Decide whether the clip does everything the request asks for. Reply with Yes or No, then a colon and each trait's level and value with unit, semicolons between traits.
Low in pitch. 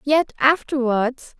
No: very high, 270 Hz